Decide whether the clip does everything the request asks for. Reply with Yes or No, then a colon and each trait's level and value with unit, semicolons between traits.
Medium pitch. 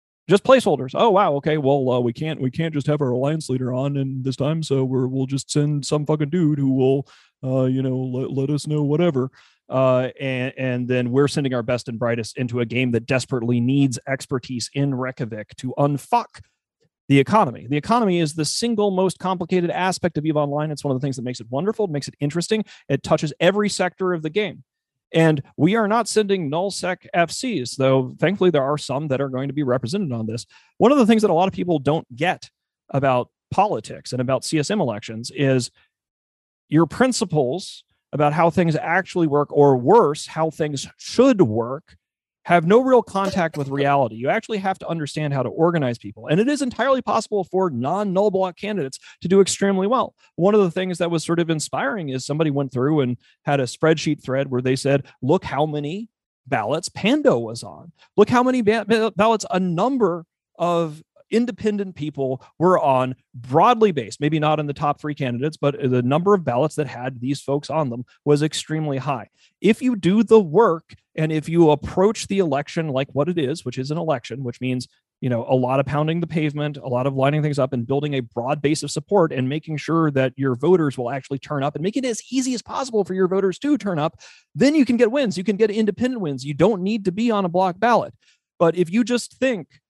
Yes: medium, 150 Hz